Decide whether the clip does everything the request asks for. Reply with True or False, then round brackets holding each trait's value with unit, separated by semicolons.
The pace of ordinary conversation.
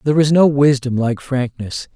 True (185 wpm)